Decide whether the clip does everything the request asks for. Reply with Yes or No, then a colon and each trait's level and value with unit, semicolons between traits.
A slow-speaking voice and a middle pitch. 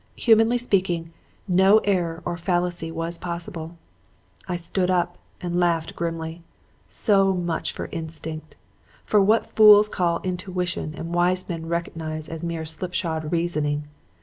Yes: slow, 130 wpm; medium, 175 Hz